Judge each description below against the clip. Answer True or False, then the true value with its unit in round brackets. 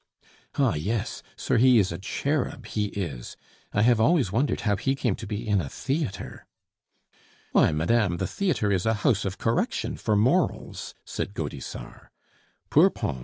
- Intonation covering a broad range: False (4.5 semitones)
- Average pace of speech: True (165 wpm)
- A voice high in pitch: False (105 Hz)